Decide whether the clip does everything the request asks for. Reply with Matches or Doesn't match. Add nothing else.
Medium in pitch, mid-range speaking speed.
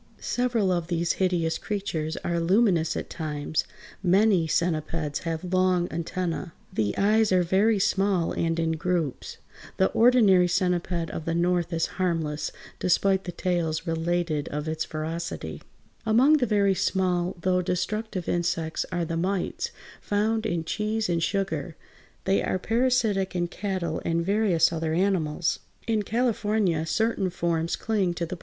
Matches